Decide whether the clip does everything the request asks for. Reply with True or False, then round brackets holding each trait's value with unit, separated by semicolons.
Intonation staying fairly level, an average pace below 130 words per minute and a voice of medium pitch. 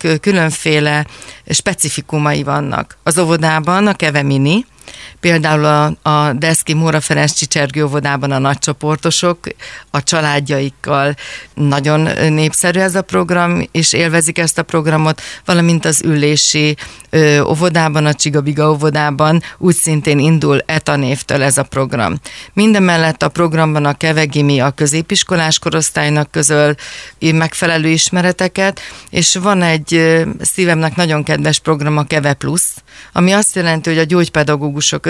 True (2.1 semitones; 120 wpm; 155 Hz)